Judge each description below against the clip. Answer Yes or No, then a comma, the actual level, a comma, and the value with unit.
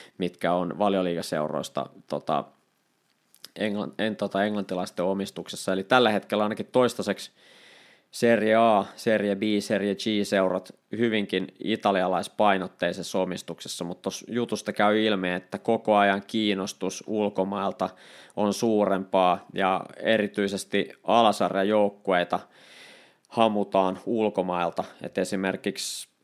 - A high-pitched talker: No, low, 100 Hz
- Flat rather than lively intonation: Yes, narrow, 2.1 semitones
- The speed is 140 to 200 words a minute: No, average, 100 wpm